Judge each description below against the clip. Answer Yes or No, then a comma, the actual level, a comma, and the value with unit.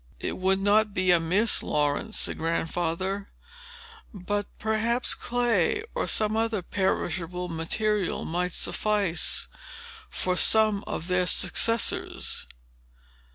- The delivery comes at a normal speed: No, slow, 105 wpm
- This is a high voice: Yes, high, 195 Hz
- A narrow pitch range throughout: No, average, 3.5 semitones